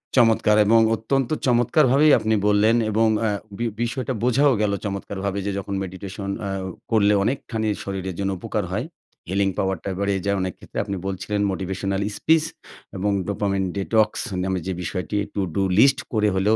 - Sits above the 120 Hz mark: No, low, 100 Hz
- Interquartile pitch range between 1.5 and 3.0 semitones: Yes, average, 2.7 semitones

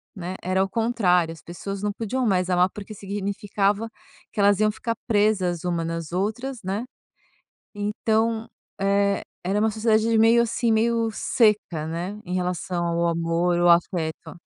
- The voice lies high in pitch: Yes, high, 200 Hz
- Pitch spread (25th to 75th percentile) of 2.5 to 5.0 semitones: Yes, average, 3.7 semitones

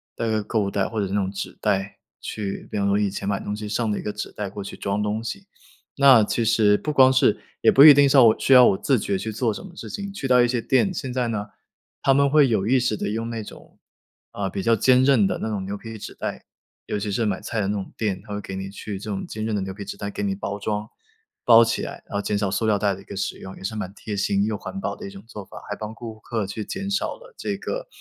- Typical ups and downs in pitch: Yes, average, 3.4 semitones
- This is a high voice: No, low, 105 Hz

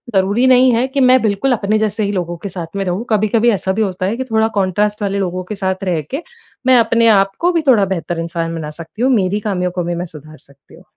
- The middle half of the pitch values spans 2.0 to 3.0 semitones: No, average, 3.9 semitones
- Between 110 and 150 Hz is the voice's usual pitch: No, high, 200 Hz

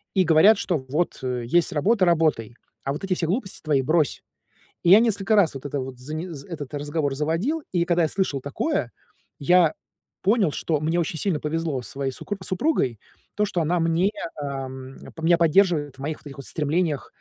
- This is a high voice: No, medium, 160 Hz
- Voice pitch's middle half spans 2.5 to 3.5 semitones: No, average, 4.4 semitones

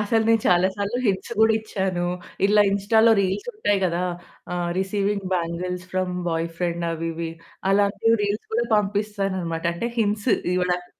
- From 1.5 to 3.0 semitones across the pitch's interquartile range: Yes, average, 2.7 semitones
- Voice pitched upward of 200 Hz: No, high, 195 Hz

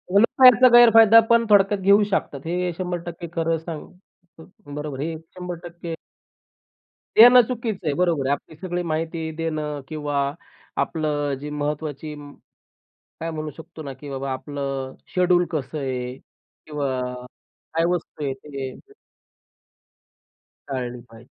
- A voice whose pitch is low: No, medium, 160 Hz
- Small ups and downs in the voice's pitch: No, average, 3.9 semitones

